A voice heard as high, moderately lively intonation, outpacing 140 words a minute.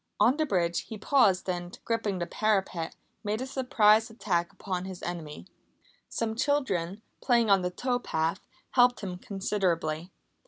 Yes: high, 195 Hz; average, 4.5 semitones; average, 150 wpm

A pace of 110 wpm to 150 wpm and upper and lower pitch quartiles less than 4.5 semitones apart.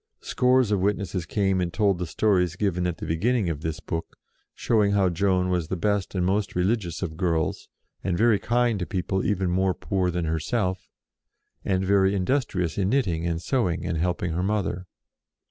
No: average, 180 wpm; average, 2.7 semitones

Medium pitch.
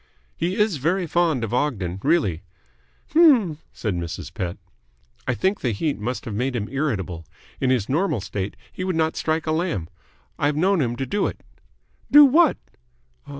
Yes: medium, 145 Hz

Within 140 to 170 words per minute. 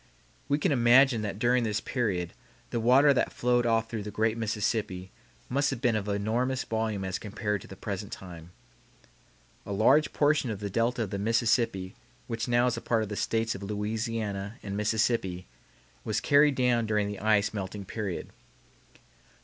No: average, 180 wpm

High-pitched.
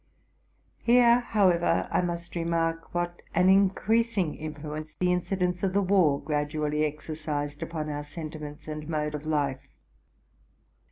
No: medium, 165 Hz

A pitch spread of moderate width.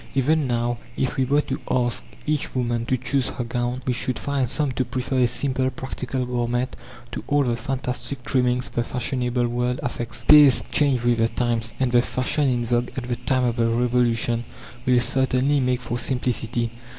No: narrow, 1.6 semitones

